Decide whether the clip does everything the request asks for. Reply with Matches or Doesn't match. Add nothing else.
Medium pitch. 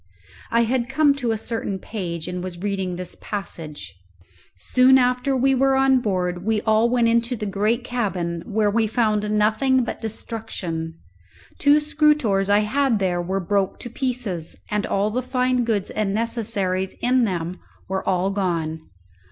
Doesn't match